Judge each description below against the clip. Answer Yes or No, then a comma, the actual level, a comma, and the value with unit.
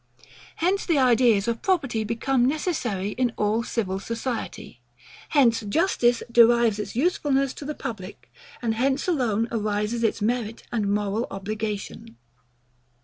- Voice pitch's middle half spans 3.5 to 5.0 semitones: Yes, average, 3.9 semitones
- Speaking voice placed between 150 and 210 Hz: No, high, 230 Hz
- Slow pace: Yes, slow, 130 wpm